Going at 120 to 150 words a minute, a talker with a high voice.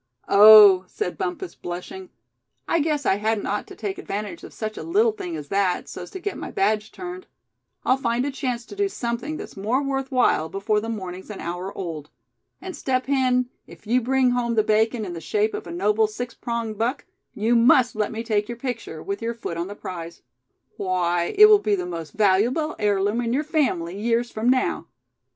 No: fast, 205 wpm; high, 220 Hz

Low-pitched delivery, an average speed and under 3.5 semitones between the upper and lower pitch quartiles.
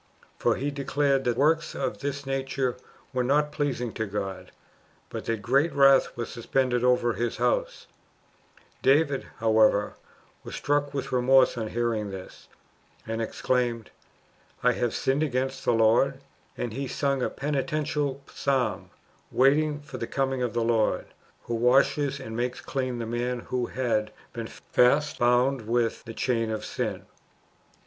Yes: low, 125 Hz; average, 150 wpm; average, 2.9 semitones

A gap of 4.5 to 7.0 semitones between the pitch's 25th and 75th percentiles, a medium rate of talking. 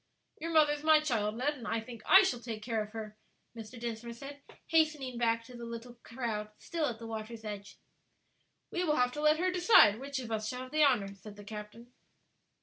No: average, 5.0 semitones; fast, 220 wpm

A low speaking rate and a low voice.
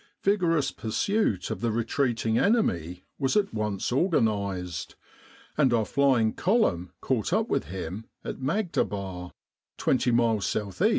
Yes: slow, 125 wpm; low, 115 Hz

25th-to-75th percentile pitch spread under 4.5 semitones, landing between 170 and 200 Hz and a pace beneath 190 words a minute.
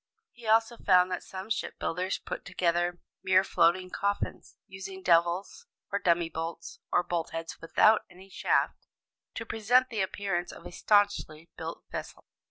Yes: average, 2.8 semitones; medium, 185 Hz; average, 160 wpm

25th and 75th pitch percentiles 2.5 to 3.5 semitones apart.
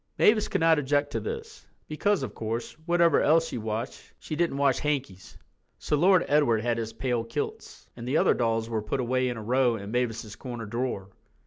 No: average, 4.9 semitones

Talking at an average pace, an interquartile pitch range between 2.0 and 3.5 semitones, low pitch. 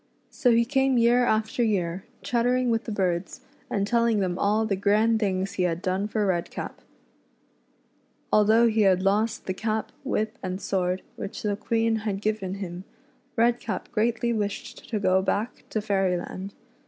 No: average, 165 wpm; average, 3.1 semitones; high, 210 Hz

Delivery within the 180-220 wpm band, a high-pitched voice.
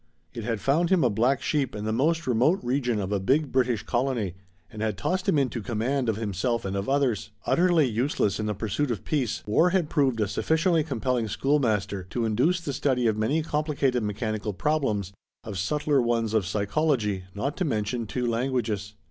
No: average, 190 wpm; low, 120 Hz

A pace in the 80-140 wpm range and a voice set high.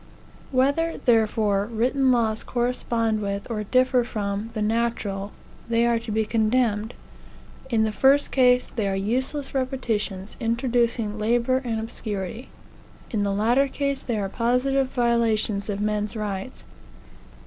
Yes: slow, 135 wpm; high, 230 Hz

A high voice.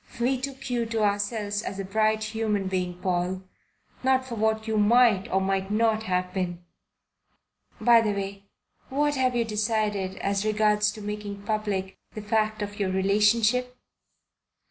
Yes: high, 210 Hz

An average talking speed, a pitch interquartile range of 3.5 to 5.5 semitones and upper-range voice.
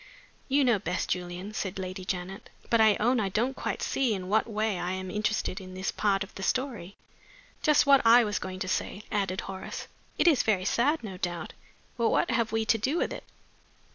No: fast, 215 wpm; average, 3.8 semitones; high, 205 Hz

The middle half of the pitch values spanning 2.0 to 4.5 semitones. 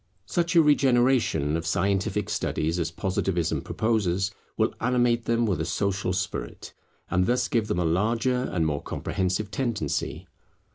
No: average, 5.2 semitones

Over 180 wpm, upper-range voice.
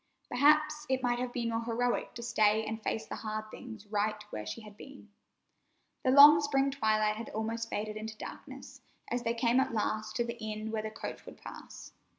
Yes: average, 200 wpm; high, 225 Hz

